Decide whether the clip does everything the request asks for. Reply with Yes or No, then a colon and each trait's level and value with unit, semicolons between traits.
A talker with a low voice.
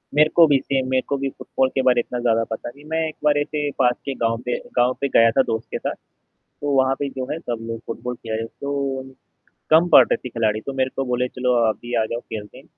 Yes: low, 130 Hz